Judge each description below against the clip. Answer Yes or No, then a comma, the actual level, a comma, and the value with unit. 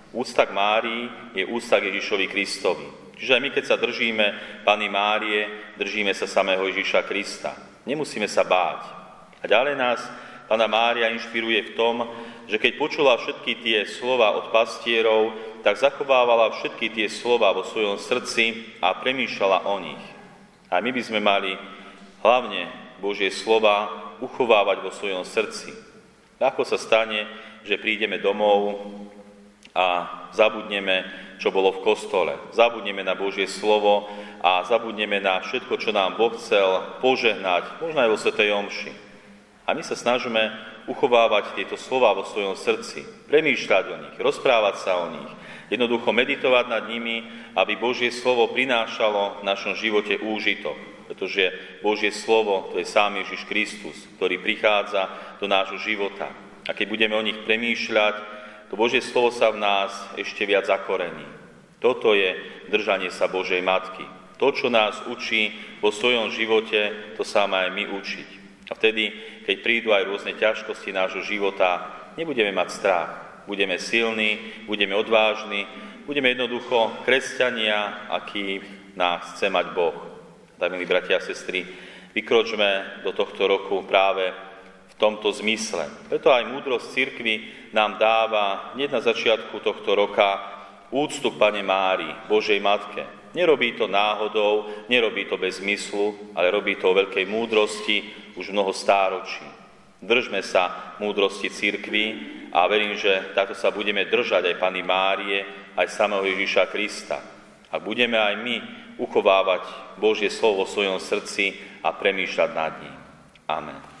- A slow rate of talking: No, average, 140 wpm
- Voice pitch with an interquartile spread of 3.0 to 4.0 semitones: No, narrow, 2.6 semitones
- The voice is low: Yes, low, 105 Hz